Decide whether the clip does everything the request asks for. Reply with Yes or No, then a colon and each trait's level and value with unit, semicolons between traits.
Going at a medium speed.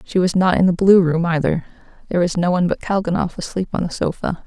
No: fast, 240 wpm